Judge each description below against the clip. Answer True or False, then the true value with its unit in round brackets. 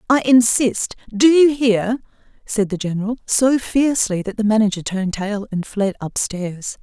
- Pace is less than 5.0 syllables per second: True (4.6 syllables/s)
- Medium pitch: False (220 Hz)